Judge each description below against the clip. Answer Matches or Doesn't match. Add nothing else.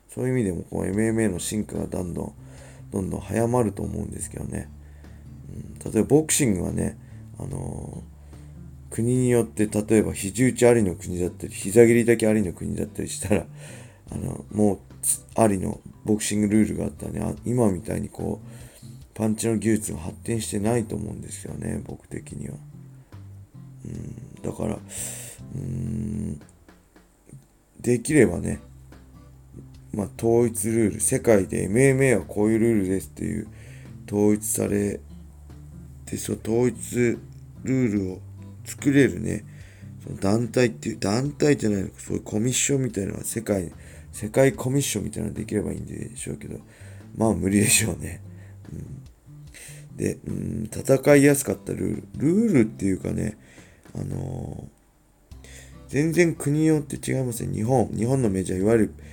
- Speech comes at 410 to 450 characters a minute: Doesn't match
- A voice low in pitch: Matches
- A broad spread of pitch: Doesn't match